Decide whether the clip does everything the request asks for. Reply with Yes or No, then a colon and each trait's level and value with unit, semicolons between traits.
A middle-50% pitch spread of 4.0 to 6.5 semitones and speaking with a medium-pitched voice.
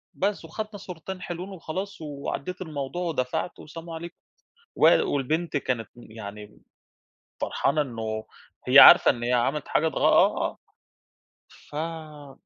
Yes: wide, 5.4 semitones; medium, 155 Hz